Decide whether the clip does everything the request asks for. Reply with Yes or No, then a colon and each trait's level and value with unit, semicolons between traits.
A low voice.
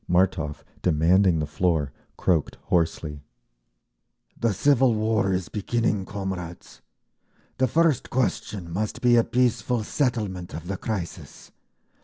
Yes: very low, 95 Hz